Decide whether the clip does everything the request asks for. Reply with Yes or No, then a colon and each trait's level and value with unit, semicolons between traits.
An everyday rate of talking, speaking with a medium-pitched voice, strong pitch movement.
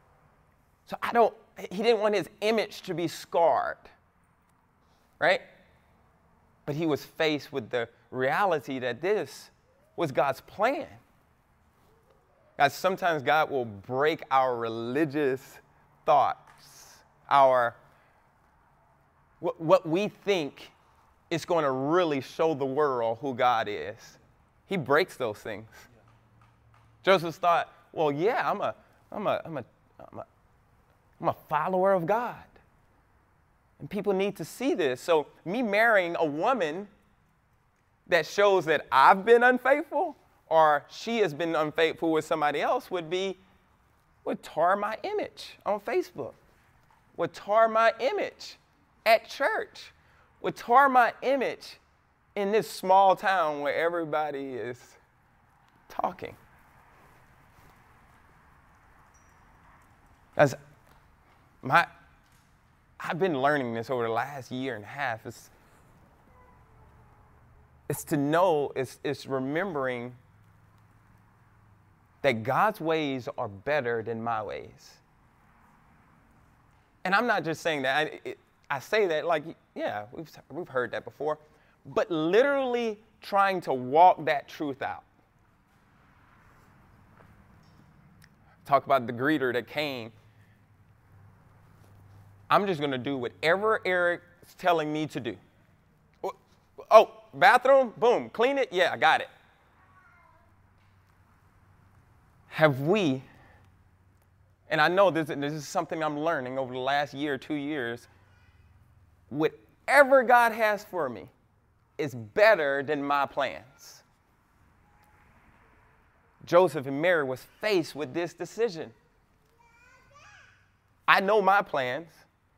No: slow, 115 wpm; medium, 145 Hz; wide, 8.4 semitones